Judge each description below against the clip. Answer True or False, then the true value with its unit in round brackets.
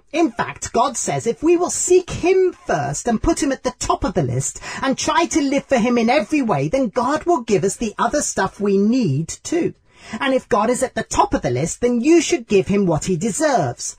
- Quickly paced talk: True (245 wpm)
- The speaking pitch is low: False (255 Hz)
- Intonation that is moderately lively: False (7.9 semitones)